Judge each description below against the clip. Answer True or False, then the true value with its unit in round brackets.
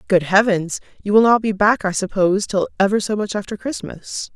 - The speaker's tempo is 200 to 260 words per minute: True (205 wpm)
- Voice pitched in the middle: False (200 Hz)